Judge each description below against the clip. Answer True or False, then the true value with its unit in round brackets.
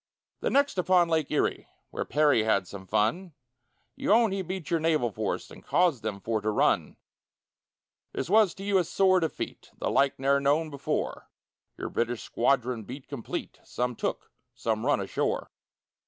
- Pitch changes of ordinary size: False (7.7 semitones)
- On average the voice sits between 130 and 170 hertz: True (140 Hz)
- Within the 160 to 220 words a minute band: True (170 wpm)